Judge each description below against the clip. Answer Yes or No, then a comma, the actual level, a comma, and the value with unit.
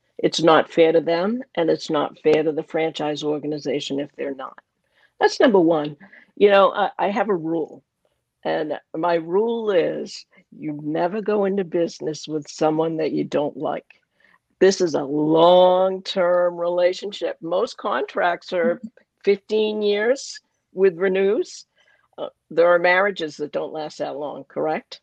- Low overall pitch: No, medium, 180 Hz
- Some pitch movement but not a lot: Yes, average, 4.2 semitones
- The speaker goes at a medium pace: Yes, average, 155 wpm